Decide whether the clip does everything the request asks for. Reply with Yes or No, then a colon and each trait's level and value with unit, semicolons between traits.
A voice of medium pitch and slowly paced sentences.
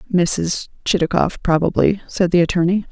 Yes: medium, 175 Hz; slow, 125 wpm